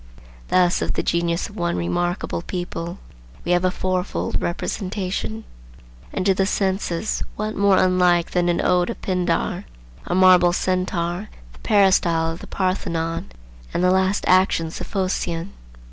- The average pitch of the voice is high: No, medium, 180 Hz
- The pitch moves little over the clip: Yes, narrow, 1.6 semitones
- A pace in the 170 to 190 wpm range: No, average, 145 wpm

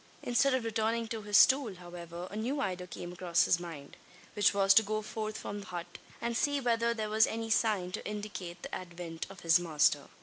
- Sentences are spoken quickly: Yes, fast, 210 wpm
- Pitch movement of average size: Yes, average, 4.3 semitones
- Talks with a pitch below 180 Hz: No, high, 205 Hz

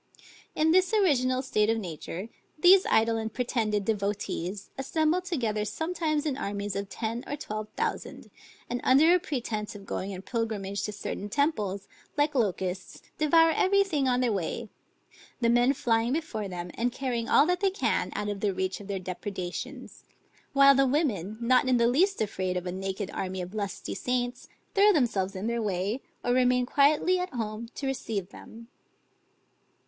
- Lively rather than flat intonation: Yes, wide, 5.7 semitones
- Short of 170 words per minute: No, average, 175 wpm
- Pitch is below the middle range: No, high, 235 Hz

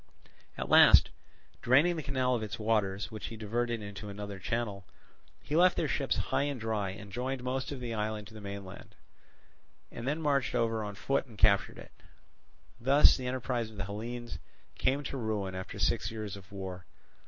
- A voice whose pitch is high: No, low, 110 Hz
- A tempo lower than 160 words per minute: No, average, 185 wpm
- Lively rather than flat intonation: No, average, 4.0 semitones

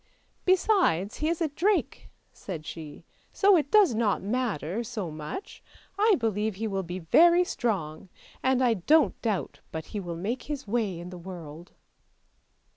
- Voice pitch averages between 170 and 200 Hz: No, high, 215 Hz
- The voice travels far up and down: Yes, wide, 8.8 semitones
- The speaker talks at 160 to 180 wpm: Yes, average, 170 wpm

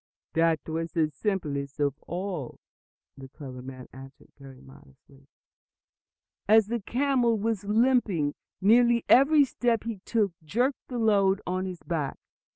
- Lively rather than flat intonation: Yes, wide, 8.0 semitones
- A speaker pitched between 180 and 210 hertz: Yes, high, 190 Hz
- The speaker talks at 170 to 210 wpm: No, slow, 135 wpm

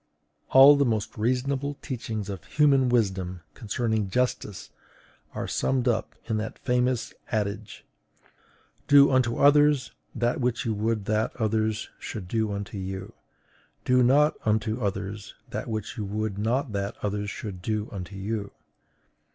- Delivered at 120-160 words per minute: Yes, average, 140 wpm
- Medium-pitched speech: No, low, 110 Hz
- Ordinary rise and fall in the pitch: Yes, average, 3.6 semitones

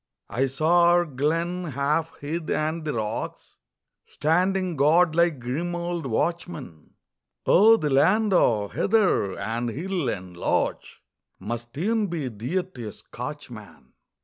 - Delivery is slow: Yes, slow, 130 wpm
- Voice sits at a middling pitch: Yes, medium, 155 Hz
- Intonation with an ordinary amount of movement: No, wide, 5.8 semitones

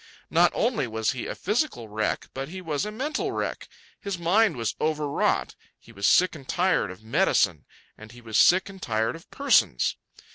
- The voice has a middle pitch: Yes, medium, 150 Hz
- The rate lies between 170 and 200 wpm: Yes, average, 185 wpm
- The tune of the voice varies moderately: No, wide, 9.0 semitones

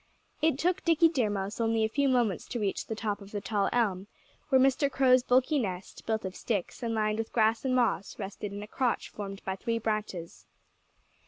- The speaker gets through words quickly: Yes, fast, 210 wpm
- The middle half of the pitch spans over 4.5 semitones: No, average, 3.9 semitones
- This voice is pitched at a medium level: No, high, 225 Hz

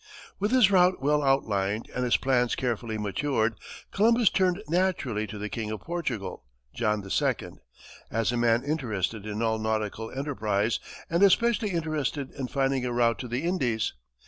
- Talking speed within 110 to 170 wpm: Yes, average, 160 wpm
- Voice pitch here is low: Yes, low, 125 Hz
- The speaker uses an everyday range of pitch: No, wide, 6.6 semitones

